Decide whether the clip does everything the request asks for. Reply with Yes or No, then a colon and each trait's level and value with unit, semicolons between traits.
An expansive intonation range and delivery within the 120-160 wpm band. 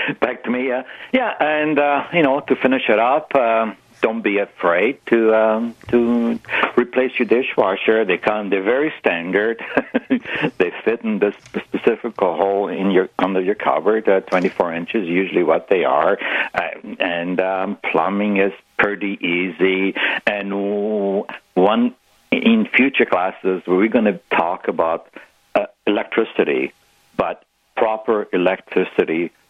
Yes: wide, 5.9 semitones; average, 140 wpm